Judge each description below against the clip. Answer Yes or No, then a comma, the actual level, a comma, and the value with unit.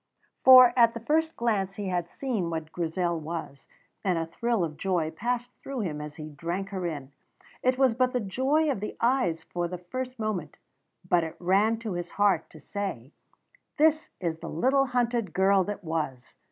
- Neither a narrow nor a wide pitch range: No, wide, 6.5 semitones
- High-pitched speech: Yes, high, 195 Hz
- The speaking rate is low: No, average, 190 wpm